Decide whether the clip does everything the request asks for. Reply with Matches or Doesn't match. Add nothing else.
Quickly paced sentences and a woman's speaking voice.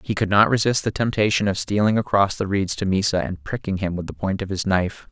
Doesn't match